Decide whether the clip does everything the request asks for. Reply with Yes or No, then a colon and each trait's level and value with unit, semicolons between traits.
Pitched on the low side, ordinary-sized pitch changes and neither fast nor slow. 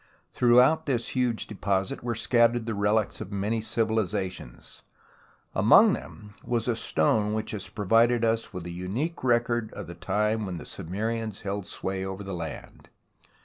Yes: low, 110 Hz; average, 3.3 semitones; average, 155 wpm